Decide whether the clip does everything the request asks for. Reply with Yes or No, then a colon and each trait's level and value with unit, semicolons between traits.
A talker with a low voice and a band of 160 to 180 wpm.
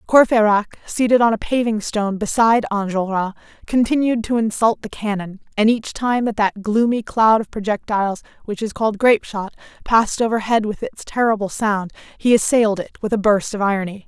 No: high, 215 Hz; average, 175 wpm